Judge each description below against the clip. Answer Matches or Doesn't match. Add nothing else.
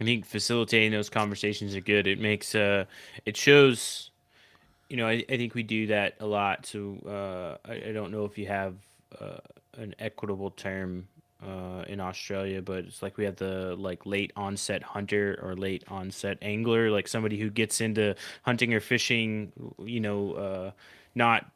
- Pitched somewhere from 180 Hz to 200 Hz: Doesn't match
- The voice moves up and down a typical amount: Doesn't match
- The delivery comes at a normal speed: Matches